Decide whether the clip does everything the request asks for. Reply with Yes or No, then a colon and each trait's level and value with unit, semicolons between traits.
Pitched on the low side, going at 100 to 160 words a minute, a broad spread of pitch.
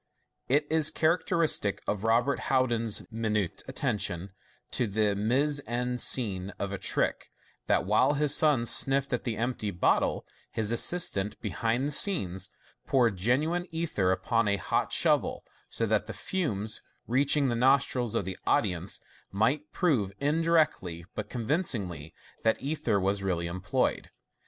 Yes: low, 115 Hz; average, 140 wpm; wide, 5.9 semitones